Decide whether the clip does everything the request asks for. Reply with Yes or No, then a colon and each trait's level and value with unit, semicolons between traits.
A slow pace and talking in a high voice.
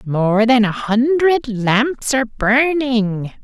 Yes: slow, 120 wpm; high, 240 Hz